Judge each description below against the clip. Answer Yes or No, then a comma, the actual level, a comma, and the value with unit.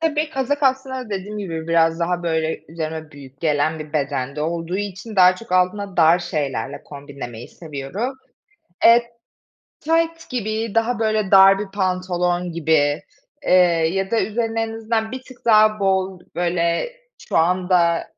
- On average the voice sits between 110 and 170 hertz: No, medium, 185 Hz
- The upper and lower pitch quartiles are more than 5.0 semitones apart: Yes, wide, 5.5 semitones